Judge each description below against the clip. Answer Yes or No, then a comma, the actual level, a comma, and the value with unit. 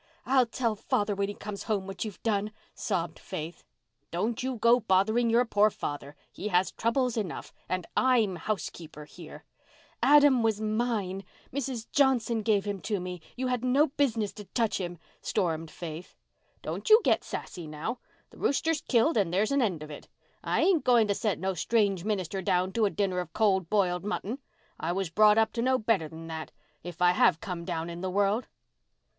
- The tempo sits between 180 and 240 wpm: Yes, average, 185 wpm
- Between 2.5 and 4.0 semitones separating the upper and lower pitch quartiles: No, average, 4.5 semitones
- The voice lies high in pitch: Yes, high, 205 Hz